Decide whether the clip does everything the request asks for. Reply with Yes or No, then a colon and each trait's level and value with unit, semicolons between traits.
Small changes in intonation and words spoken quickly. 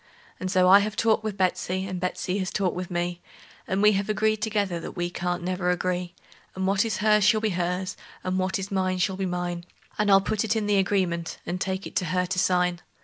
Yes: narrow, 2.1 semitones; fast, 235 wpm